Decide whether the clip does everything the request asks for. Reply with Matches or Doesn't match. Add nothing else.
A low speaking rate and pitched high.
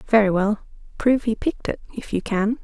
Doesn't match